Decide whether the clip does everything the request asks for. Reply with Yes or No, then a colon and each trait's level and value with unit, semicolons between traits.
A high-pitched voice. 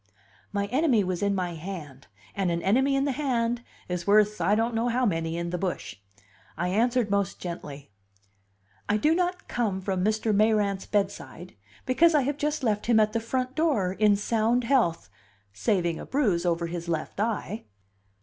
Yes: high, 210 Hz